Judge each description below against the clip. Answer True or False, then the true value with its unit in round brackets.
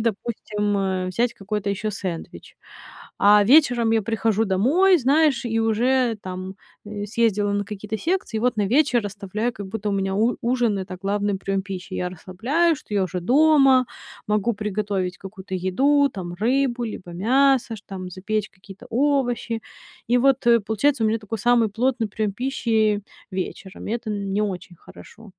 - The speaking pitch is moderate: False (215 Hz)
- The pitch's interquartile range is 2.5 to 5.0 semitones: True (3.6 semitones)